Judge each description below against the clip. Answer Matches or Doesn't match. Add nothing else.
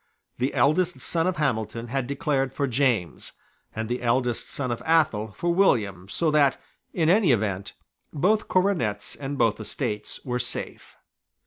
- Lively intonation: Matches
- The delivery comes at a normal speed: Matches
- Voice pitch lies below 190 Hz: Matches